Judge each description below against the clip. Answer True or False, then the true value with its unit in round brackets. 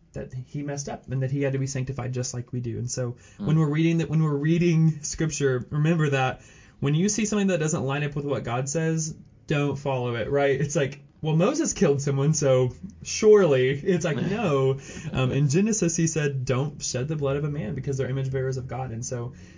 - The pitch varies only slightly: False (3.5 semitones)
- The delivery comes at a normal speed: False (225 wpm)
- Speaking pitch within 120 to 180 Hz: True (140 Hz)